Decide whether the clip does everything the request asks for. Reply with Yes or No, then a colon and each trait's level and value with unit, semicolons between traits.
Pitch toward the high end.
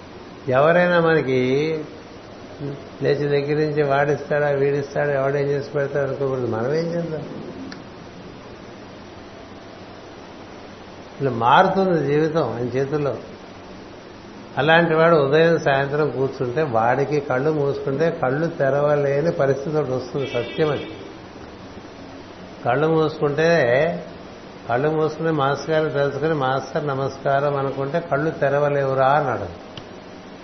No: medium, 140 Hz